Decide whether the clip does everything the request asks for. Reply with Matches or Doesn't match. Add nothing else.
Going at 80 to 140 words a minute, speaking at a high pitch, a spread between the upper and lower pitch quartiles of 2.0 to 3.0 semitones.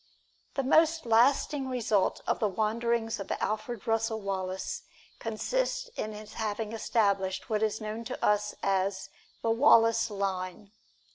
Matches